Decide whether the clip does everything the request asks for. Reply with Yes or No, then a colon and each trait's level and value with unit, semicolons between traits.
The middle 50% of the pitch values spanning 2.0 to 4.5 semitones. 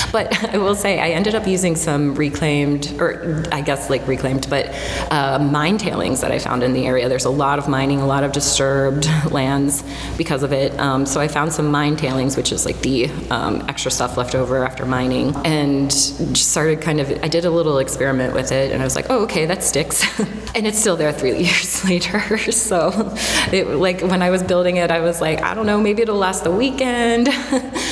No: average, 5.1 semitones